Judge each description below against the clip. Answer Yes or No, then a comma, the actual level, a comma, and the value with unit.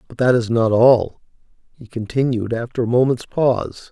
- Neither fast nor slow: Yes, average, 170 wpm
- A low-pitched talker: Yes, low, 120 Hz